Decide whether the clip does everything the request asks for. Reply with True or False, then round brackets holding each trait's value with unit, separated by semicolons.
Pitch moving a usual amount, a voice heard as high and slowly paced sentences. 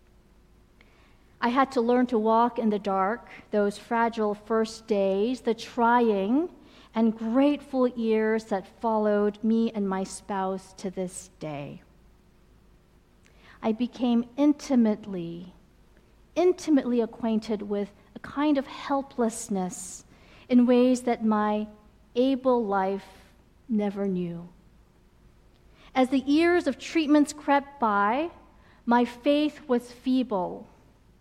True (4.0 semitones; 230 Hz; 110 wpm)